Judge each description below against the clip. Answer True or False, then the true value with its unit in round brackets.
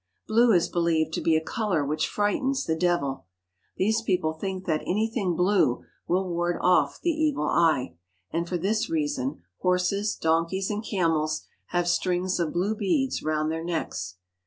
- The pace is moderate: True (160 wpm)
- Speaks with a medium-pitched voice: True (175 Hz)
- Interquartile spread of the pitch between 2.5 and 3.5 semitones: False (4.2 semitones)